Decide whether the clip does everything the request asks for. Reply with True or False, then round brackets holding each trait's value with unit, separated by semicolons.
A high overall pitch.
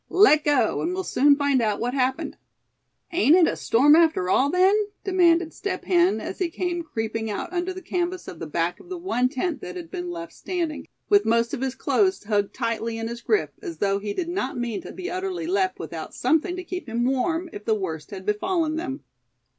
True (320 Hz)